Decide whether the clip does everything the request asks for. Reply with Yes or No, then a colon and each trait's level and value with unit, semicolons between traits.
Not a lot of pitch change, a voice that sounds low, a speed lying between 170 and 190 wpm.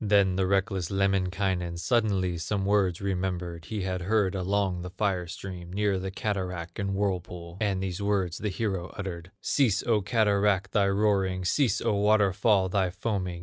No: narrow, 2.0 semitones; very low, 95 Hz; average, 160 wpm